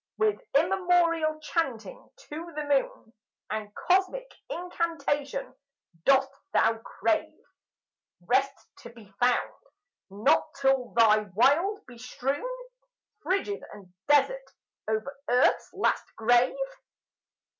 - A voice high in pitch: Yes, very high, 280 Hz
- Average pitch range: No, wide, 6.3 semitones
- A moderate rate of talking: No, slow, 100 wpm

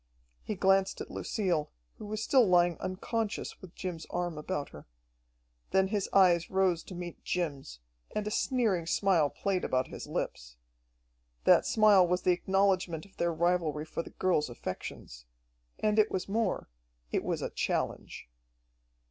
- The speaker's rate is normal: Yes, average, 155 wpm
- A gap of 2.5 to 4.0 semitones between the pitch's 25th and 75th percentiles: Yes, average, 3.0 semitones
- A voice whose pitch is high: No, medium, 180 Hz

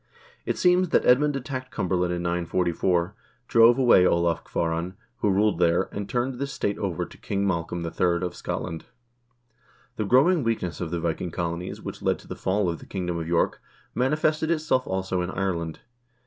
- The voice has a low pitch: Yes, very low, 95 Hz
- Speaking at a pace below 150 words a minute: No, average, 180 wpm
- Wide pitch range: Yes, wide, 6.1 semitones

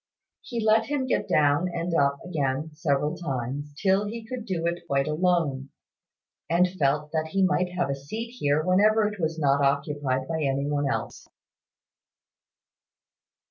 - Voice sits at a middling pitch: Yes, medium, 160 Hz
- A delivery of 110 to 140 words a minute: No, average, 155 wpm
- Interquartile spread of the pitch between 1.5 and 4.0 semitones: No, average, 4.7 semitones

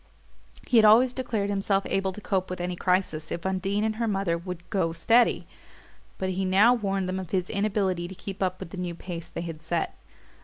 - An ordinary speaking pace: No, fast, 215 wpm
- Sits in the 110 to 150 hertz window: No, high, 190 Hz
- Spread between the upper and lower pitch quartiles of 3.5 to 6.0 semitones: No, narrow, 2.4 semitones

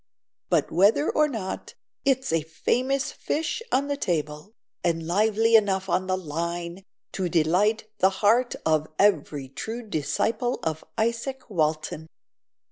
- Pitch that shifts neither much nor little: No, wide, 6.1 semitones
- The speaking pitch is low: No, high, 190 Hz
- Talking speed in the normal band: No, slow, 130 wpm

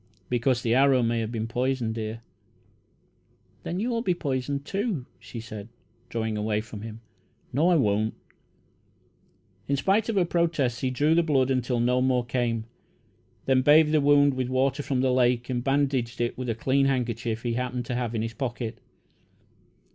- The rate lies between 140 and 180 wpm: Yes, average, 175 wpm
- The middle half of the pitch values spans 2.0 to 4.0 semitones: Yes, average, 3.2 semitones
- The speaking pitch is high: No, low, 125 Hz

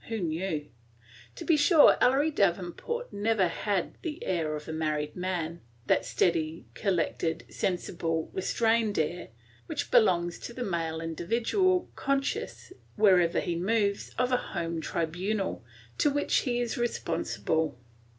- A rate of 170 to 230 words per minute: No, slow, 135 wpm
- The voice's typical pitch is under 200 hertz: Yes, medium, 185 Hz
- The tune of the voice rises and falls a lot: Yes, wide, 6.0 semitones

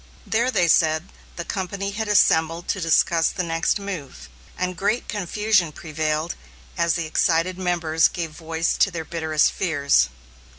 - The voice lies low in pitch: No, medium, 170 Hz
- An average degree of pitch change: Yes, average, 3.0 semitones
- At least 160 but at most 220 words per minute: No, average, 145 wpm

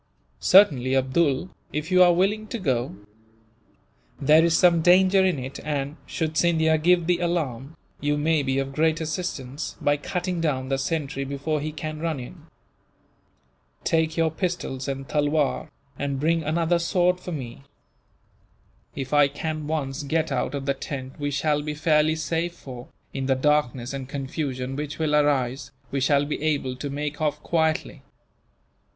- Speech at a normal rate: Yes, average, 160 wpm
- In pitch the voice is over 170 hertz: No, medium, 150 Hz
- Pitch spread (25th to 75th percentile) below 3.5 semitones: Yes, average, 3.1 semitones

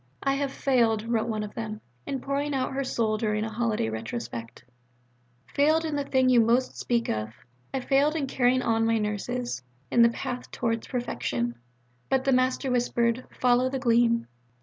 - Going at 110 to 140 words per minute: No, average, 170 wpm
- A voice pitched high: Yes, high, 240 Hz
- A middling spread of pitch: Yes, average, 3.0 semitones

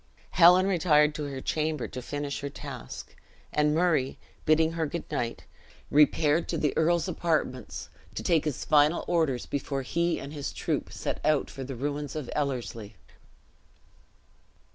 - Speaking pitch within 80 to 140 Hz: No, medium, 150 Hz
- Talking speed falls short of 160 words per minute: Yes, average, 150 wpm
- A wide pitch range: No, average, 2.7 semitones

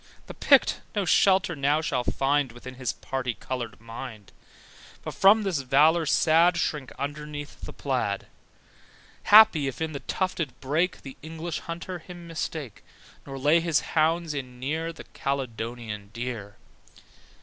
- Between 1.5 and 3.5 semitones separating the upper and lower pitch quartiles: No, average, 4.6 semitones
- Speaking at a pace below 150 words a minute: Yes, average, 140 wpm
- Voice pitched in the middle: Yes, medium, 145 Hz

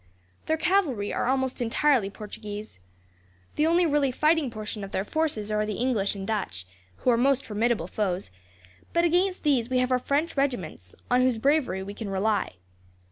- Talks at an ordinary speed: Yes, average, 175 wpm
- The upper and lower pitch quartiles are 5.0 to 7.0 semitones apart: Yes, wide, 5.6 semitones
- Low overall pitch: No, high, 240 Hz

